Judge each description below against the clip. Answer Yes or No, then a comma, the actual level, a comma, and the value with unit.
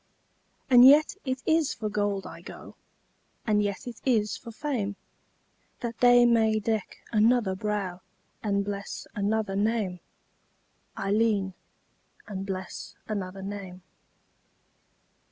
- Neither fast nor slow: No, slow, 115 wpm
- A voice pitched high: Yes, high, 210 Hz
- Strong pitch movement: No, average, 2.9 semitones